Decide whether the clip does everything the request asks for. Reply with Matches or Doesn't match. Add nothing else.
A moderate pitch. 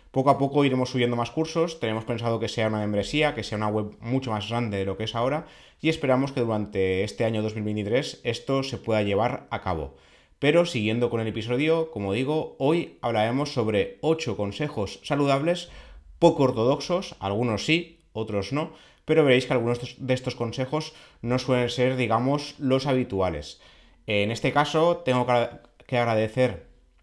Doesn't match